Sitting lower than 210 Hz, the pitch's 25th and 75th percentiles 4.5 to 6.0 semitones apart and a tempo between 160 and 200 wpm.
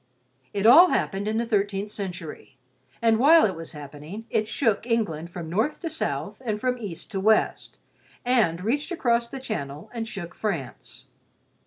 No: high, 215 Hz; average, 5.3 semitones; average, 165 wpm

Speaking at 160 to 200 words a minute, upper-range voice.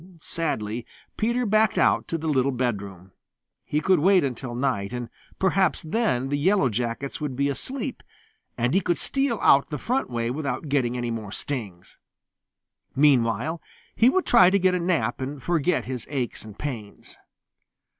No: average, 165 wpm; medium, 140 Hz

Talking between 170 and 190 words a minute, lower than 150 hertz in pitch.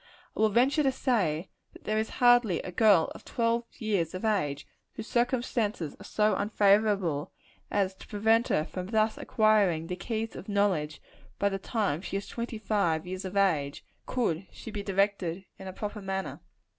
No: average, 180 wpm; high, 200 Hz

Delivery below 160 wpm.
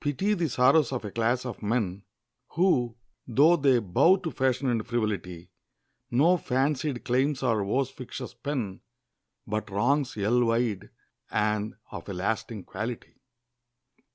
Yes: average, 140 wpm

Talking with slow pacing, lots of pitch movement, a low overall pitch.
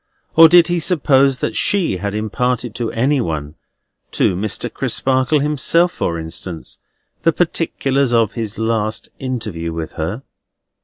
Yes: slow, 125 wpm; wide, 6.1 semitones; low, 120 Hz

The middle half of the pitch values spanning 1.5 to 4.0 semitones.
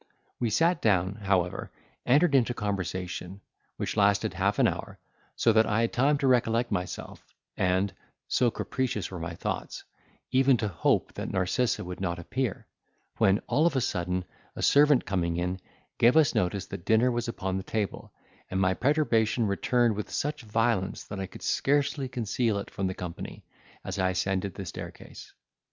No: average, 5.0 semitones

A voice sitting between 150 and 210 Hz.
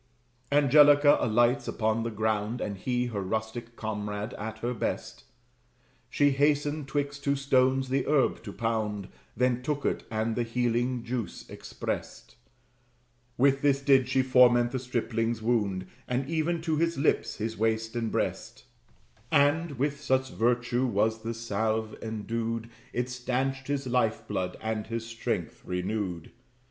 No: low, 120 Hz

